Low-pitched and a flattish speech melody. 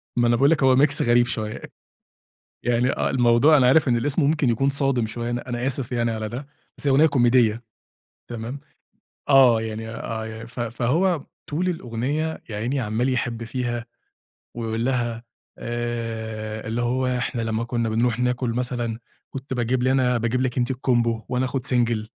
Yes: low, 120 Hz; narrow, 2.0 semitones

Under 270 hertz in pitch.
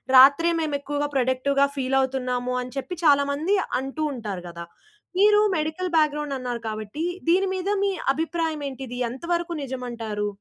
No: very high, 275 Hz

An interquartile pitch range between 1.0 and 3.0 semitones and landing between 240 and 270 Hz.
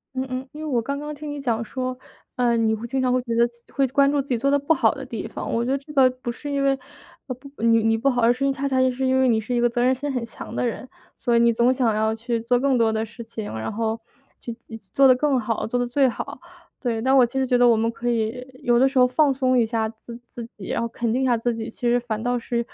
Yes: narrow, 2.4 semitones; high, 245 Hz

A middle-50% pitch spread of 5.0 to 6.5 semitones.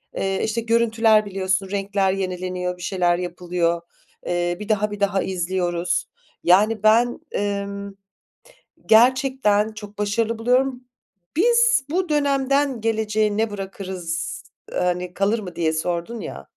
No: average, 3.9 semitones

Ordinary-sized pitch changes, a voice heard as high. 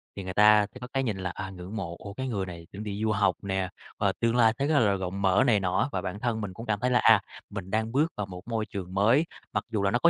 No: average, 3.1 semitones; low, 105 Hz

